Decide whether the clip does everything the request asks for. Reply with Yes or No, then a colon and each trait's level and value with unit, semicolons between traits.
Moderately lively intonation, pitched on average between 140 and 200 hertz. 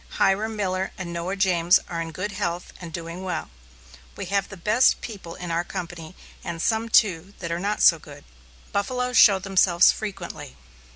Yes: average, 3.0 semitones; medium, 185 Hz